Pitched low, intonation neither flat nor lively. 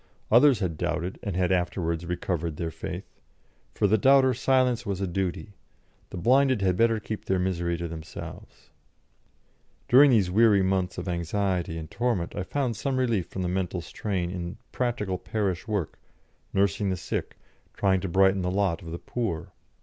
Yes: very low, 95 Hz; average, 4.0 semitones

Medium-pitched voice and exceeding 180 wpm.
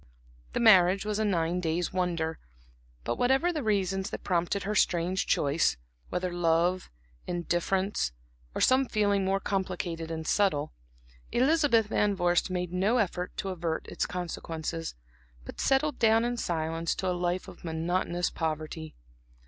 No: medium, 180 Hz; average, 145 wpm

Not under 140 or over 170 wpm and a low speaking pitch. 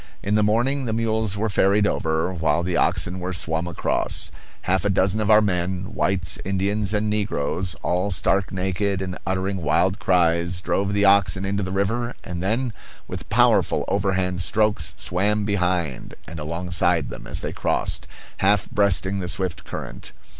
Yes: average, 165 wpm; very low, 95 Hz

